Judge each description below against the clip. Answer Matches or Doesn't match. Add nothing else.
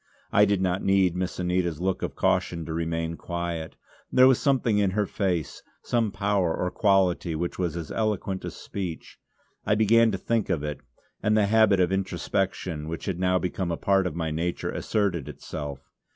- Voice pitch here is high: Doesn't match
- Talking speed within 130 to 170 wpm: Doesn't match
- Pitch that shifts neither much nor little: Matches